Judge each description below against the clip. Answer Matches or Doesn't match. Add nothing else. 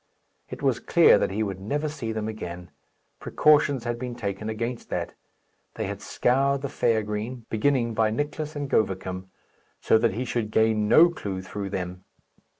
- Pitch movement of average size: Matches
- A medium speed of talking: Matches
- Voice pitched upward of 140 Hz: Doesn't match